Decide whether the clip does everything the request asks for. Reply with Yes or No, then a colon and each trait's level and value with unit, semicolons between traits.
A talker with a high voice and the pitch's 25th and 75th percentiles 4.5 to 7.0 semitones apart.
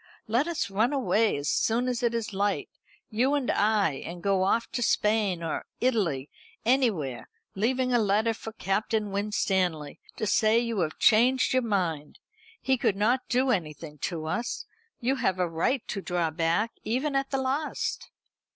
Yes: high, 215 Hz; average, 5.2 semitones